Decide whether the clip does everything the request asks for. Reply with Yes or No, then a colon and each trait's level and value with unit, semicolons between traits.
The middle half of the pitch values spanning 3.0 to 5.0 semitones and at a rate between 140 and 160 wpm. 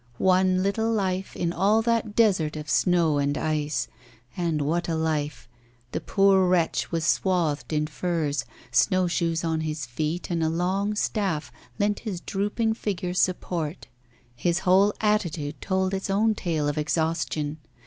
Yes: average, 3.8 semitones; average, 150 wpm